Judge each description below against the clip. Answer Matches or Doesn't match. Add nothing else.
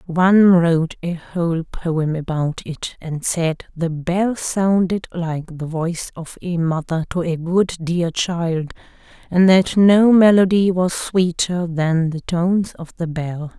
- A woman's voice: Matches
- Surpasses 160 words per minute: Doesn't match